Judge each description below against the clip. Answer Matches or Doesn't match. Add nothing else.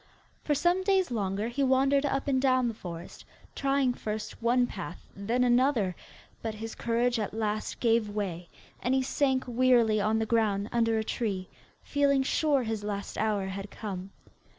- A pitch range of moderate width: Matches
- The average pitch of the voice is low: Doesn't match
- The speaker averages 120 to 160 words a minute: Doesn't match